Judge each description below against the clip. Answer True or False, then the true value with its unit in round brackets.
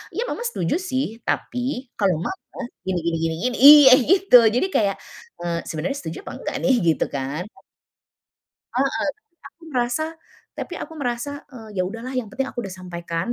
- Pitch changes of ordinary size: False (7.3 semitones)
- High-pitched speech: True (235 Hz)